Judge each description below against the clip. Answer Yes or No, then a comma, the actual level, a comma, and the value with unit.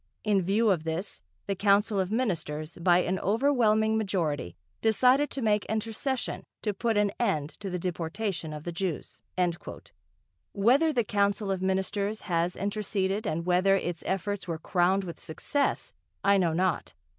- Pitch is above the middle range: Yes, high, 195 Hz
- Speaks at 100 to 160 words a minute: Yes, average, 155 wpm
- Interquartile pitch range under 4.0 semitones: Yes, average, 3.6 semitones